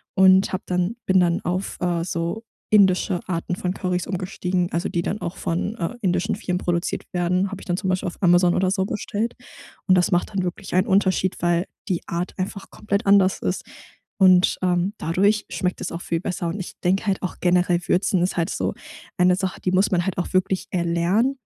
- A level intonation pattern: Yes, narrow, 1.6 semitones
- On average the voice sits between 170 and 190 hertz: Yes, medium, 185 Hz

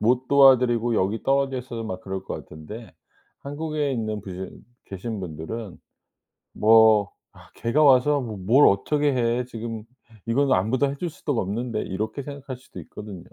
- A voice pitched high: No, low, 115 Hz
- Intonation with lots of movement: No, average, 4.4 semitones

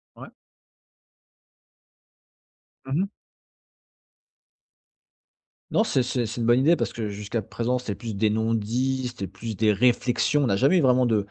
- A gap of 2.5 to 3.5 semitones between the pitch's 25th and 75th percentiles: Yes, average, 3.1 semitones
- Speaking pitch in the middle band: No, low, 120 Hz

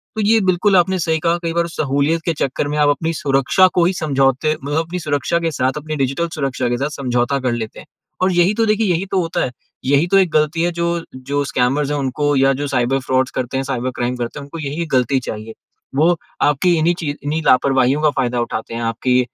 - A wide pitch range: No, average, 4.3 semitones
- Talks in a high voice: No, medium, 145 Hz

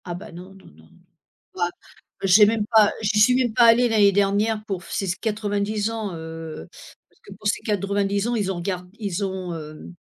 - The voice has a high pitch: Yes, high, 200 Hz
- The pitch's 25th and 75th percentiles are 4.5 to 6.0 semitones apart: No, average, 2.9 semitones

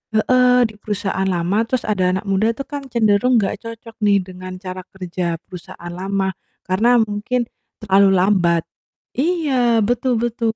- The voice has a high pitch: Yes, high, 210 Hz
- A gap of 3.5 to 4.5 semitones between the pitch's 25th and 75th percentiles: Yes, average, 4.0 semitones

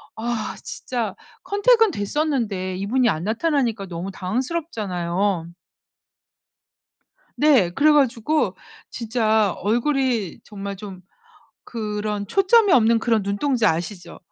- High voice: Yes, high, 220 Hz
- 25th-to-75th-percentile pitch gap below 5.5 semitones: Yes, average, 5.1 semitones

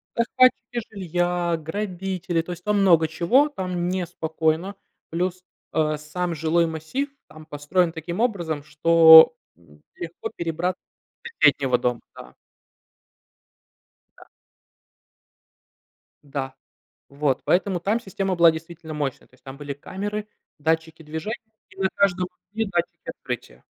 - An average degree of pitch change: Yes, average, 3.2 semitones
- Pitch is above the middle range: No, medium, 170 Hz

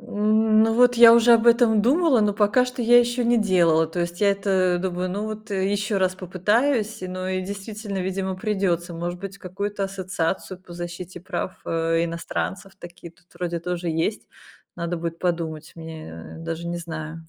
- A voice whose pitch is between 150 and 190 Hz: Yes, medium, 185 Hz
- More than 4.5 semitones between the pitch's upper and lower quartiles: No, average, 3.7 semitones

